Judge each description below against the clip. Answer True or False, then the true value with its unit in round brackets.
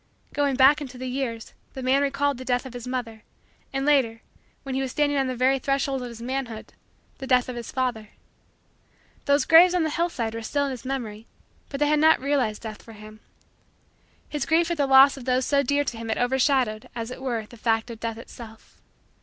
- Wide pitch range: False (3.2 semitones)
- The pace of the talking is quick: True (220 wpm)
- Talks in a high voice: True (260 Hz)